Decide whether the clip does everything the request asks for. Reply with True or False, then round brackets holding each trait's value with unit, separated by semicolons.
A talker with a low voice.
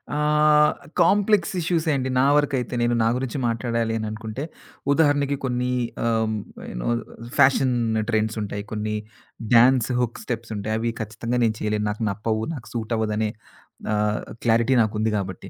True (115 Hz)